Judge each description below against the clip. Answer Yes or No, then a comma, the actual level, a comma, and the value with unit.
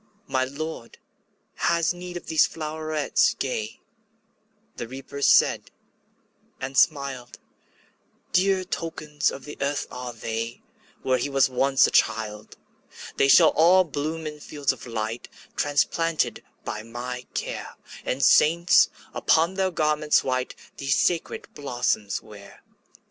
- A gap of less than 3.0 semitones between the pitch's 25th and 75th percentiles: No, average, 4.1 semitones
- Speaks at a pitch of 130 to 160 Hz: Yes, medium, 140 Hz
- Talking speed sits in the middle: No, slow, 125 wpm